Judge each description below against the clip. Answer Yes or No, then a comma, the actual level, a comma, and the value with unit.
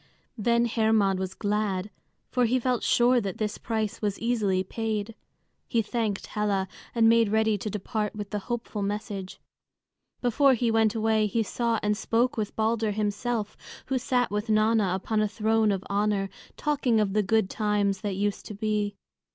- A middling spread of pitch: No, narrow, 2.0 semitones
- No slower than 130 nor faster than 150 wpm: No, average, 170 wpm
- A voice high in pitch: Yes, high, 215 Hz